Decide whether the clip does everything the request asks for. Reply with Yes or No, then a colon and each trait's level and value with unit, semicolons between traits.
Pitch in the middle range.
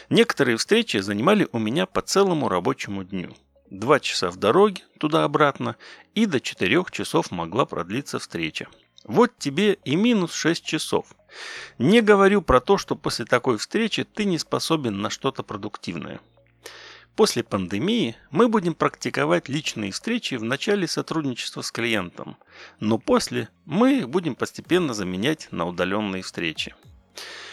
Yes: medium, 160 Hz